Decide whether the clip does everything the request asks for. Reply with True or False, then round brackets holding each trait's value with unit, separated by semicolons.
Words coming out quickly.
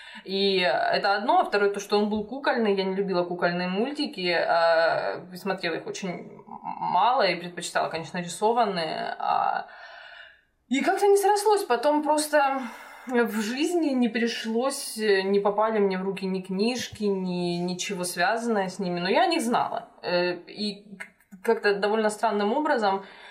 False (140 wpm)